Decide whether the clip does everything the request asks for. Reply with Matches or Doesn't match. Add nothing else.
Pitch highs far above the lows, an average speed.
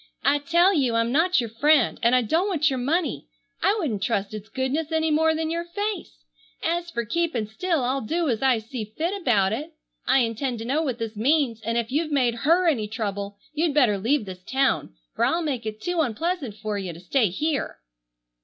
Doesn't match